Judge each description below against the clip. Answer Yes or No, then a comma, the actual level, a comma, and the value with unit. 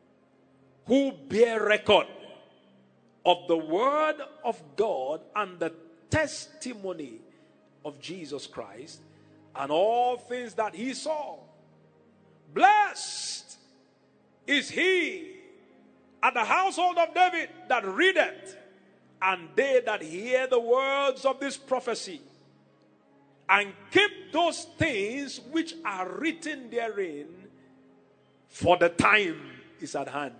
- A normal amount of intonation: No, wide, 8.4 semitones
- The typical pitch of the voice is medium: No, very high, 265 Hz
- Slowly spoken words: Yes, slow, 105 wpm